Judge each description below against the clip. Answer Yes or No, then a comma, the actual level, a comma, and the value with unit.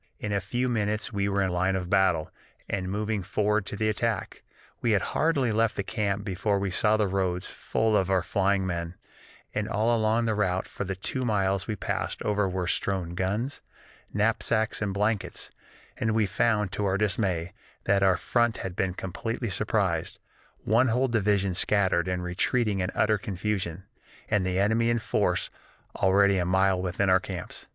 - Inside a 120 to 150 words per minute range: No, average, 180 wpm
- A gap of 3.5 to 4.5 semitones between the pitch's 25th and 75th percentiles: No, narrow, 2.6 semitones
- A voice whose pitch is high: No, low, 100 Hz